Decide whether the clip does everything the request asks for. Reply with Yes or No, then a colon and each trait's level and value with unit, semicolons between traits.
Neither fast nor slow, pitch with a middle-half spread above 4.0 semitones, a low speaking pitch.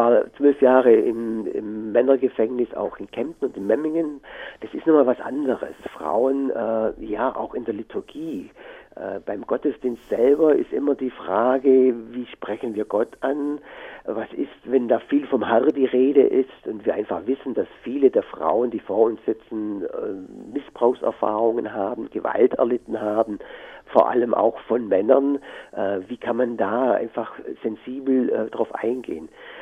Yes: average, 160 wpm; average, 4.7 semitones; low, 130 Hz